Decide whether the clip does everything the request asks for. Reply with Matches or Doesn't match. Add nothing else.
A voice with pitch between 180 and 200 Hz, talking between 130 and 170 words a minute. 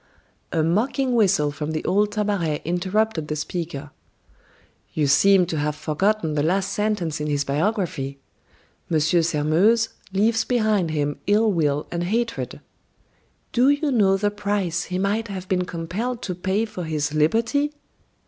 Matches